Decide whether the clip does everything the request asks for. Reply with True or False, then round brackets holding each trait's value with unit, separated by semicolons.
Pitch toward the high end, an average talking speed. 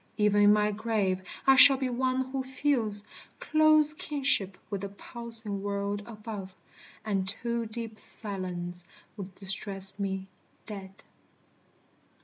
False (210 Hz; 125 wpm)